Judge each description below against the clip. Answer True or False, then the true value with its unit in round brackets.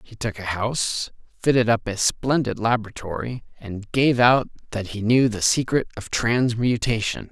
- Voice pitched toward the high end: False (115 Hz)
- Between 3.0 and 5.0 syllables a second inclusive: True (4.6 syllables/s)